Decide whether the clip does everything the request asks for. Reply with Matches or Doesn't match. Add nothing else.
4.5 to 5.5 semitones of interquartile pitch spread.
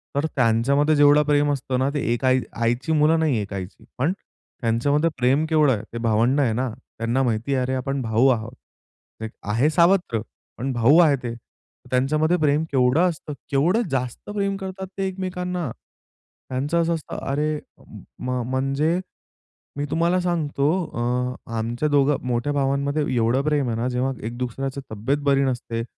Doesn't match